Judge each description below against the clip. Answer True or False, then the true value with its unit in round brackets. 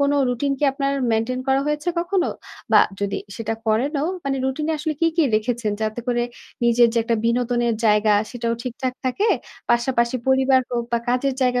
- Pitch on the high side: True (250 Hz)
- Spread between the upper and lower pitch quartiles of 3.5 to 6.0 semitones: False (2.8 semitones)